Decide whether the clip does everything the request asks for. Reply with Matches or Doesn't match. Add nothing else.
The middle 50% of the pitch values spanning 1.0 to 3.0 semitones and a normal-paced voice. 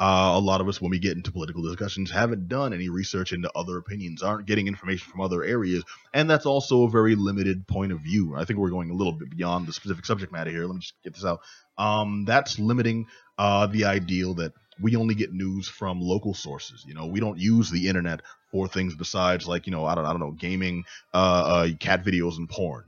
Doesn't match